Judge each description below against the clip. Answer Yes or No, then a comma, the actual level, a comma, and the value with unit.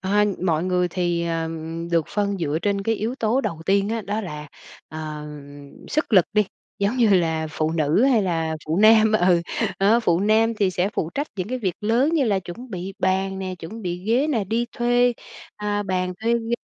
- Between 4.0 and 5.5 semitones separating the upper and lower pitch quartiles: Yes, average, 4.6 semitones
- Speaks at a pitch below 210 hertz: Yes, high, 195 Hz